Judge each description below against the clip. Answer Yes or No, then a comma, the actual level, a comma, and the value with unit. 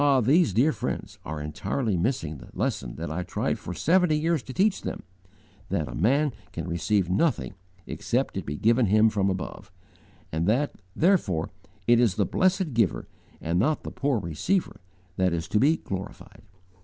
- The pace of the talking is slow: No, average, 175 wpm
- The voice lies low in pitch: Yes, low, 110 Hz